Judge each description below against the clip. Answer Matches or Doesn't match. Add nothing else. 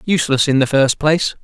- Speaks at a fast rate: Matches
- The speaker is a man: Matches